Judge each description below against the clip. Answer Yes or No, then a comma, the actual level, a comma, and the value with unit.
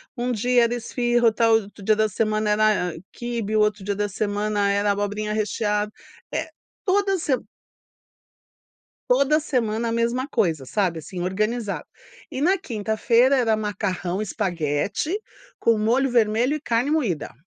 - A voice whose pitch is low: No, high, 215 Hz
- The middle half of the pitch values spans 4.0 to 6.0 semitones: No, average, 2.9 semitones